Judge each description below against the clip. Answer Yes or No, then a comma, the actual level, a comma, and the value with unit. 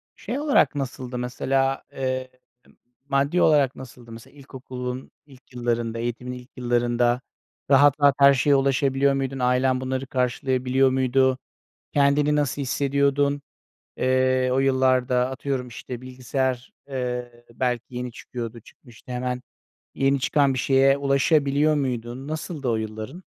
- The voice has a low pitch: Yes, low, 130 Hz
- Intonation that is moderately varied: No, narrow, 1.8 semitones